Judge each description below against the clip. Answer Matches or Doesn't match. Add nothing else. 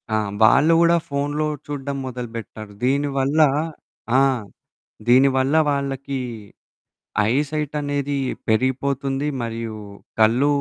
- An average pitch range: Doesn't match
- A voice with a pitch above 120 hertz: Matches